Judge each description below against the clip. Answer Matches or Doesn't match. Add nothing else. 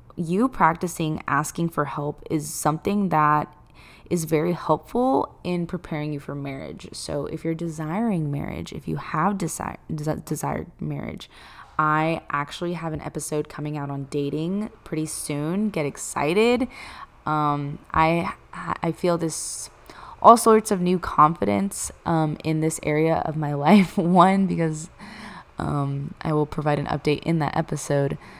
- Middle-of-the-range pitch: Matches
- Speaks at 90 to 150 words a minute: Matches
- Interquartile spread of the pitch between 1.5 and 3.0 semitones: Matches